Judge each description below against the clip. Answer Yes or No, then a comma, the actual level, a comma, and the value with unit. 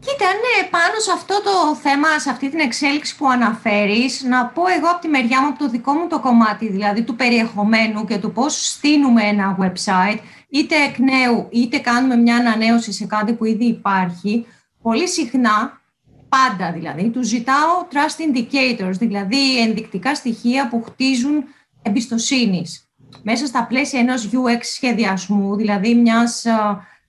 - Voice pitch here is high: Yes, high, 240 Hz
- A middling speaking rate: Yes, average, 155 wpm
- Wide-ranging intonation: No, average, 4.2 semitones